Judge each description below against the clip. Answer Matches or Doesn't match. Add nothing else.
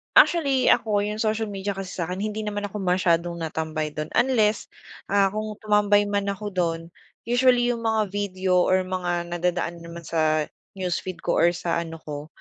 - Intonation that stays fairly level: Doesn't match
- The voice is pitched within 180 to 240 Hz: Matches